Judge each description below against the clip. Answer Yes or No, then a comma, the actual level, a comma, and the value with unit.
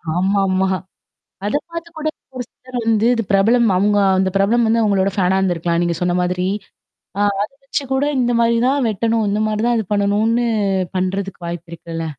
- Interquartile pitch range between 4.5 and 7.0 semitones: No, average, 3.8 semitones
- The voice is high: Yes, high, 205 Hz